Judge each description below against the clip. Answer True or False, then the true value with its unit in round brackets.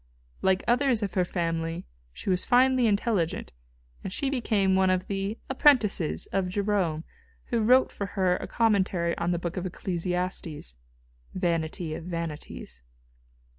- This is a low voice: False (185 Hz)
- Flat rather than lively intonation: False (3.9 semitones)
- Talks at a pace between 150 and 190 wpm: False (140 wpm)